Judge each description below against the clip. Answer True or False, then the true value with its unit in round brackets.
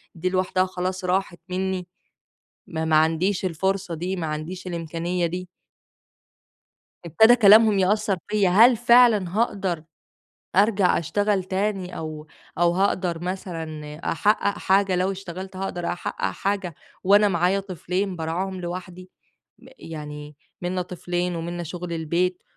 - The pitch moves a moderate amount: False (2.2 semitones)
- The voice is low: False (185 Hz)